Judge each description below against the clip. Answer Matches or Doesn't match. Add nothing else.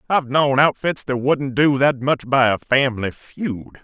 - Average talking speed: Matches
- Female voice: Doesn't match